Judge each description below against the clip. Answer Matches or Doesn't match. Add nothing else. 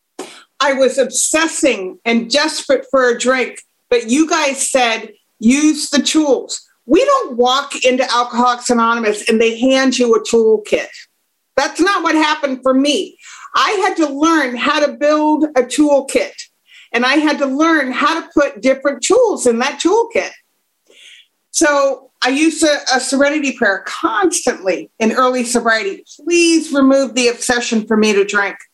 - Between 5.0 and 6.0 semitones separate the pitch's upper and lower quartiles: Doesn't match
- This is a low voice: Doesn't match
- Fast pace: Doesn't match